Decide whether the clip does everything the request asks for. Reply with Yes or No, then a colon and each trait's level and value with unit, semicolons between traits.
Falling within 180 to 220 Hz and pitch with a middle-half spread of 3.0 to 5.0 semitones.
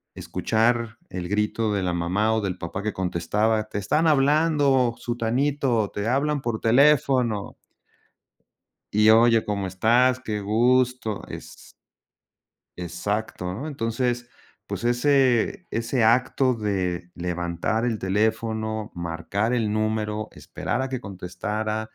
No: low, 110 Hz; average, 3.4 semitones